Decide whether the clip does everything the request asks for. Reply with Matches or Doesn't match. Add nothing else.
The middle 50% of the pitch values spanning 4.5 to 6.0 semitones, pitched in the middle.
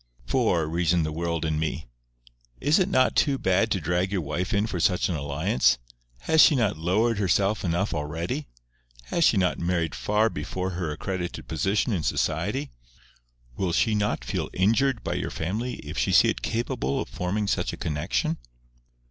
Doesn't match